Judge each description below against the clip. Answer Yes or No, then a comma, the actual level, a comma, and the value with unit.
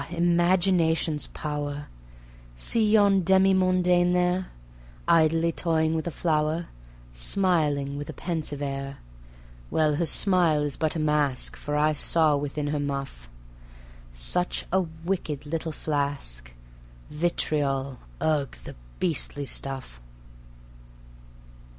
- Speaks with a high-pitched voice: No, medium, 155 Hz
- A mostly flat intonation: No, average, 3.3 semitones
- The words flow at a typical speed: No, slow, 110 wpm